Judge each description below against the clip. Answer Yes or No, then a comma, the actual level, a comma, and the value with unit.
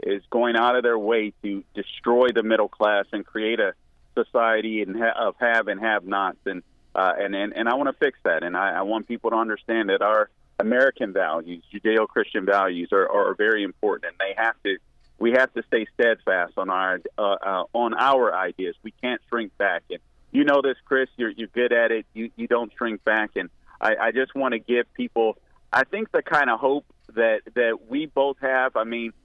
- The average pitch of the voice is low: Yes, low, 115 Hz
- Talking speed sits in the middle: No, fast, 215 wpm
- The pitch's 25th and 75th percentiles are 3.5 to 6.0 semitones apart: No, average, 3.1 semitones